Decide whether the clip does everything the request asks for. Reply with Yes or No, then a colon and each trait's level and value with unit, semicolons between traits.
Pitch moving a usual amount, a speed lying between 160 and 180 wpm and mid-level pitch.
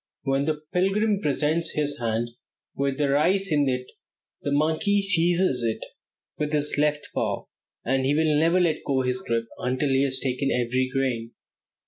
Yes: average, 3.6 semitones; average, 165 wpm; medium, 145 Hz